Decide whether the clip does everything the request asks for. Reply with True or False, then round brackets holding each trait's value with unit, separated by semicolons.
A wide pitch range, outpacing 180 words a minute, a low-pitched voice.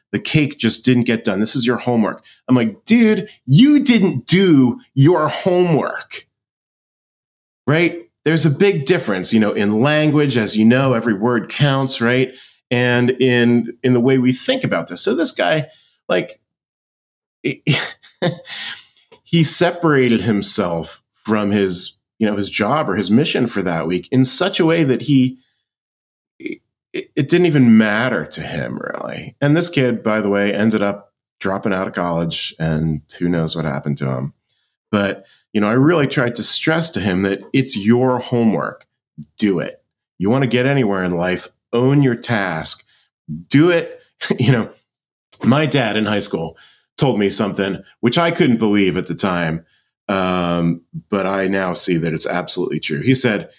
False (6.2 semitones; 170 wpm; 120 Hz)